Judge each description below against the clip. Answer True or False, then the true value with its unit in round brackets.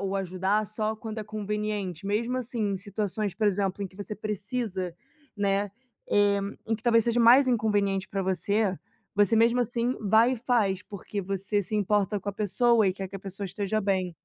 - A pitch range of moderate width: False (2.1 semitones)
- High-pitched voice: True (205 Hz)